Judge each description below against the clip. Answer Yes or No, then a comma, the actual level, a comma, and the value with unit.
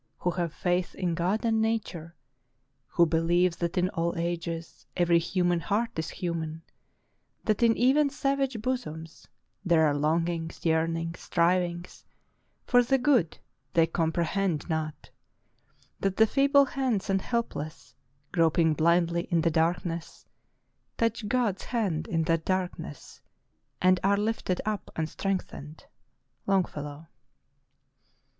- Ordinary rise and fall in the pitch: Yes, average, 4.0 semitones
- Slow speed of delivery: Yes, slow, 125 wpm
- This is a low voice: No, medium, 175 Hz